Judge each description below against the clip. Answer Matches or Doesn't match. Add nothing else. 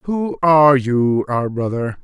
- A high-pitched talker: Doesn't match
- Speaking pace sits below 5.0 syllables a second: Matches